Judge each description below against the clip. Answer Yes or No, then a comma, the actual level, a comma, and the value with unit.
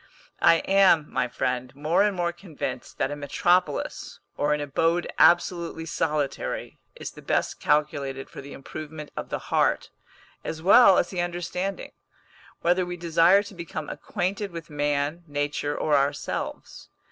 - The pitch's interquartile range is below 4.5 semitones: Yes, average, 3.4 semitones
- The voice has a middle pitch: Yes, medium, 160 Hz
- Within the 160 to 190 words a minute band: No, average, 145 wpm